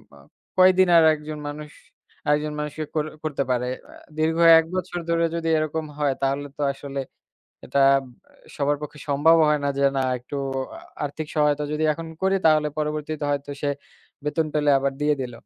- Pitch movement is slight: Yes, narrow, 1.6 semitones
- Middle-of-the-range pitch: Yes, medium, 150 Hz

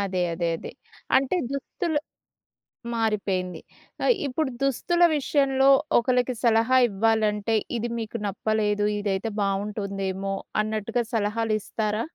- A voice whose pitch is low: No, high, 220 Hz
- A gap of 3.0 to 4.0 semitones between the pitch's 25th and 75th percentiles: Yes, average, 3.7 semitones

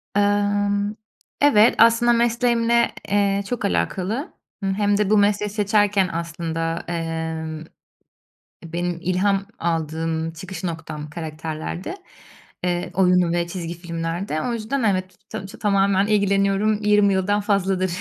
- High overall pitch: Yes, high, 195 Hz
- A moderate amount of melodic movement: Yes, average, 3.6 semitones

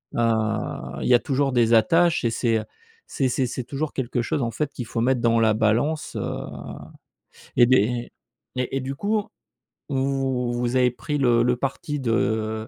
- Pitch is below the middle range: Yes, low, 125 Hz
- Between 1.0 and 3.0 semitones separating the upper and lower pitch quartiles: Yes, average, 2.7 semitones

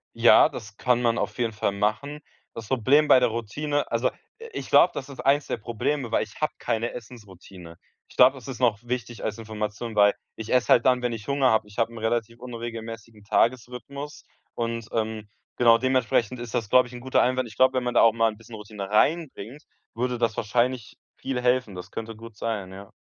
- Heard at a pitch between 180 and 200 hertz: No, low, 115 Hz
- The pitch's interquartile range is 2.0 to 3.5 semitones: Yes, average, 2.7 semitones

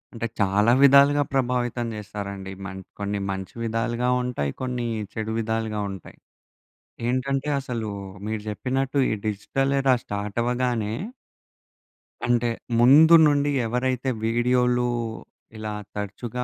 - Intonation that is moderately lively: Yes, average, 3.2 semitones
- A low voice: Yes, low, 120 Hz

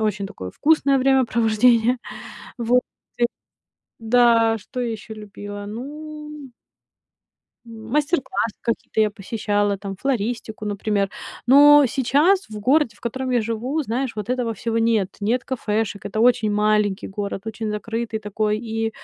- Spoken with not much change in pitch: No, average, 3.1 semitones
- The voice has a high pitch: Yes, high, 225 Hz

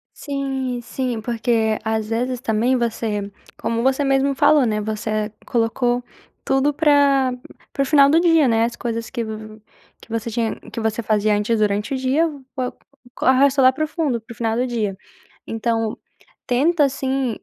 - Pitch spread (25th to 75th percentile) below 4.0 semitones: Yes, average, 3.4 semitones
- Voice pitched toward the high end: Yes, high, 240 Hz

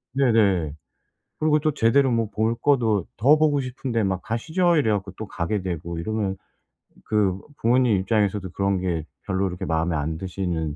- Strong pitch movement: No, average, 4.9 semitones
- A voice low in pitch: Yes, low, 105 Hz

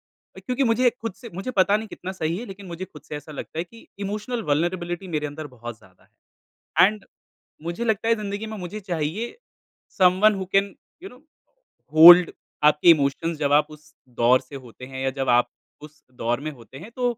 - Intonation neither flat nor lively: No, wide, 6.0 semitones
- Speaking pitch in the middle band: Yes, medium, 175 Hz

